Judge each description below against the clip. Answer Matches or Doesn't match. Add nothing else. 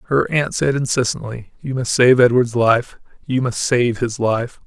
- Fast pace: Doesn't match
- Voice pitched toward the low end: Matches